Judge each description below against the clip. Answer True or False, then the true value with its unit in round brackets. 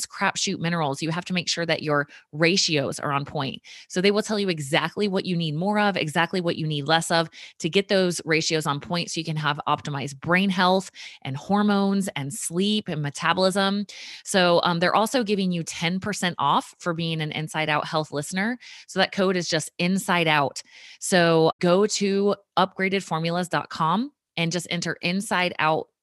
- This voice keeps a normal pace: True (185 wpm)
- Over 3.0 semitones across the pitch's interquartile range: True (3.5 semitones)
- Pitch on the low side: False (175 Hz)